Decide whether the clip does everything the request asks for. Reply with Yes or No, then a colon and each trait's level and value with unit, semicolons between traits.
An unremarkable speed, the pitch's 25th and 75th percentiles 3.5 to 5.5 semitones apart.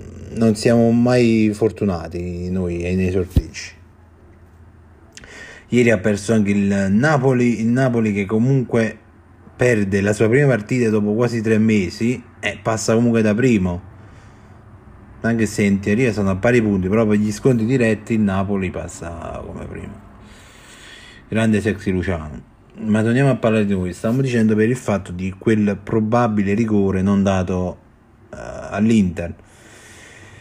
No: average, 140 wpm; average, 2.7 semitones